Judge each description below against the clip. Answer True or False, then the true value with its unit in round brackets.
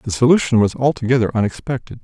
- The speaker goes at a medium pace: True (150 wpm)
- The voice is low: True (120 Hz)